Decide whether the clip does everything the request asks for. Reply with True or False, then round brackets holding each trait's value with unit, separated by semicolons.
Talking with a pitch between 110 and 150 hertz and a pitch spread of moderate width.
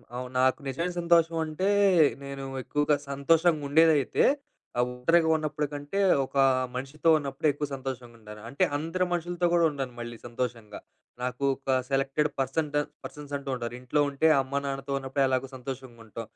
True (140 Hz; 3.1 semitones)